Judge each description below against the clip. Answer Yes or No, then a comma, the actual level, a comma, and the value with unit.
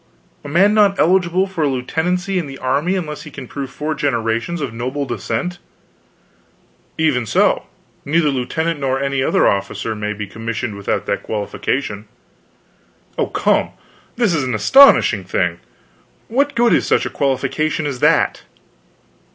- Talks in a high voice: No, medium, 140 Hz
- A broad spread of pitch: Yes, wide, 6.5 semitones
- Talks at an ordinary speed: Yes, average, 150 wpm